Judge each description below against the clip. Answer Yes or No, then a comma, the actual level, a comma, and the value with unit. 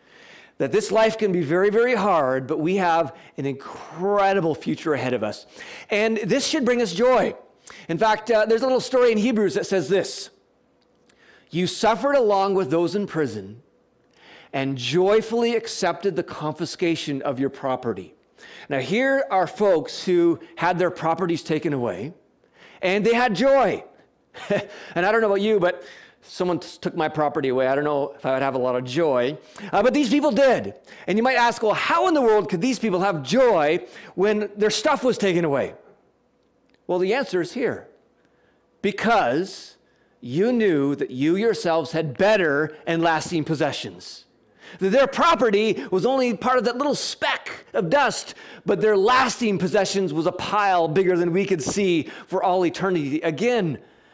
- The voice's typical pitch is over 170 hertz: Yes, high, 190 Hz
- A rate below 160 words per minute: No, average, 175 wpm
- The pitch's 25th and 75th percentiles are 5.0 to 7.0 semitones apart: Yes, average, 5.3 semitones